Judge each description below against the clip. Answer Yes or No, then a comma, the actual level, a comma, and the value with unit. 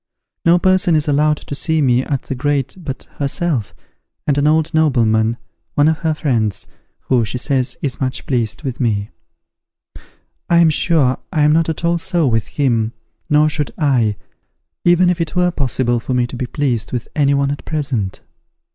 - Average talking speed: Yes, average, 180 wpm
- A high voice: No, medium, 140 Hz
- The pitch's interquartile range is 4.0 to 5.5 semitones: Yes, average, 4.3 semitones